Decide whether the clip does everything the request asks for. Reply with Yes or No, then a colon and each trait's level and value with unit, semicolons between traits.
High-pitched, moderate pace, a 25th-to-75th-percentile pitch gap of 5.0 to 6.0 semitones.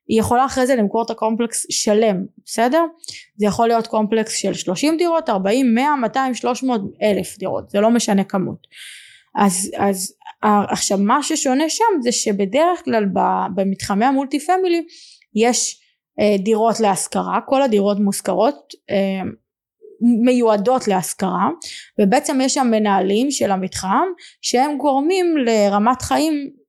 Yes: high, 235 Hz; average, 130 wpm; wide, 5.5 semitones